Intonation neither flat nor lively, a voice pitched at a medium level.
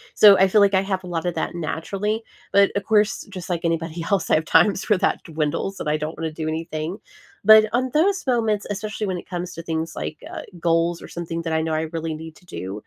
Yes: average, 3.9 semitones; medium, 175 Hz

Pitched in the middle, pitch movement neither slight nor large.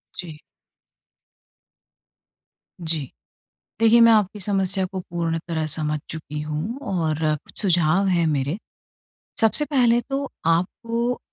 No: medium, 180 Hz; wide, 5.9 semitones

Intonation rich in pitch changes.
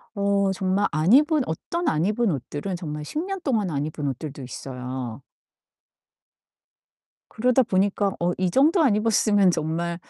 Yes: wide, 6.4 semitones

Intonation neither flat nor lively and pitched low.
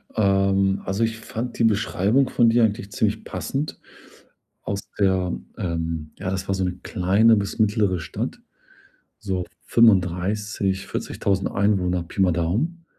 Yes: average, 3.2 semitones; low, 100 Hz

